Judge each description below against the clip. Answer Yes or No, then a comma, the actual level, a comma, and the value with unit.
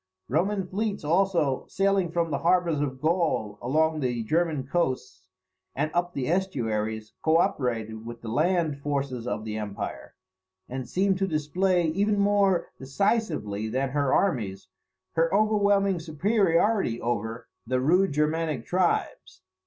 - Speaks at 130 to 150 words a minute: Yes, slow, 135 wpm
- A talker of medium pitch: Yes, medium, 155 Hz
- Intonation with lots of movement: Yes, wide, 6.8 semitones